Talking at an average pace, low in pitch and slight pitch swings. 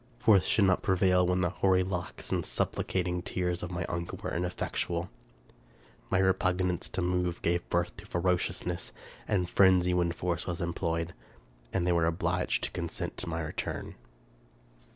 Yes: average, 160 wpm; very low, 90 Hz; narrow, 1.2 semitones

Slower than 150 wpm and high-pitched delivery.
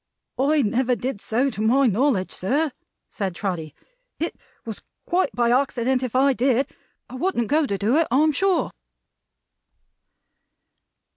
Yes: average, 140 wpm; very high, 255 Hz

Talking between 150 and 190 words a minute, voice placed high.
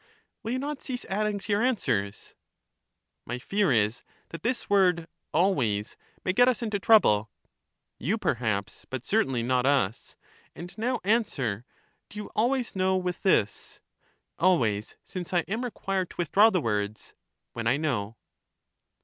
No: average, 160 wpm; medium, 180 Hz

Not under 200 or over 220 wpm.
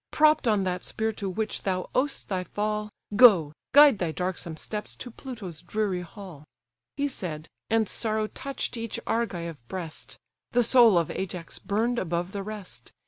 No: average, 160 wpm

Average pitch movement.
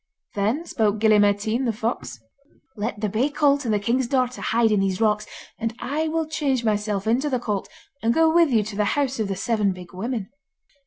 Yes: average, 3.9 semitones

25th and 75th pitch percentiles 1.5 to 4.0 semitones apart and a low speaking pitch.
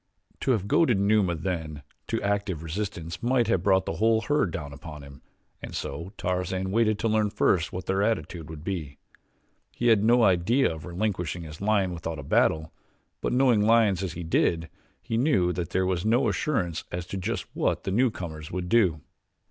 No: average, 4.6 semitones; very low, 95 Hz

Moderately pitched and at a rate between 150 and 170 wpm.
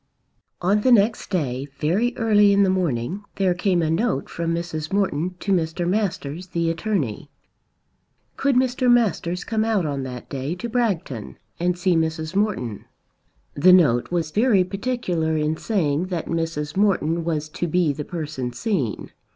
Yes: medium, 175 Hz; average, 160 wpm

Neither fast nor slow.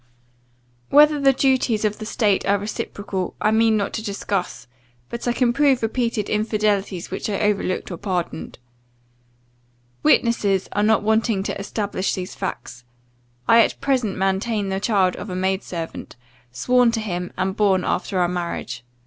Yes: average, 155 wpm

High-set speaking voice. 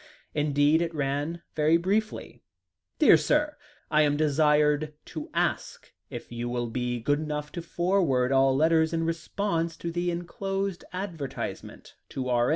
No: medium, 155 Hz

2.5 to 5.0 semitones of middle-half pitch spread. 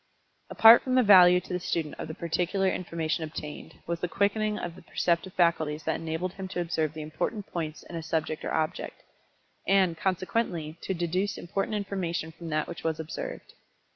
Yes: average, 2.9 semitones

